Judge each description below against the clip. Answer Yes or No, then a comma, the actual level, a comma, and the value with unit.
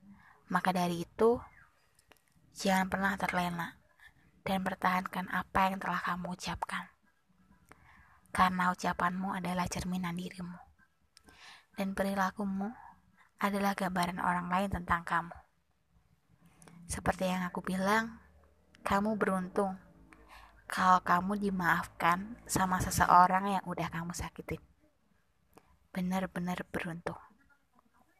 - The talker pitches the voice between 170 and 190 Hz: Yes, medium, 185 Hz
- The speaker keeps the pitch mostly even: Yes, narrow, 1.6 semitones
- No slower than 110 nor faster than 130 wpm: No, average, 90 wpm